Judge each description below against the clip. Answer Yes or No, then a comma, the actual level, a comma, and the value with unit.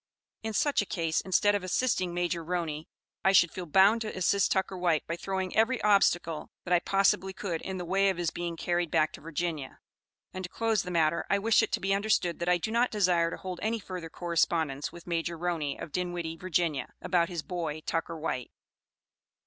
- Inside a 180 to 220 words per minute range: Yes, fast, 205 wpm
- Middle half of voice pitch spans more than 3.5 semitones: No, narrow, 2.6 semitones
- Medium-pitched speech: Yes, medium, 175 Hz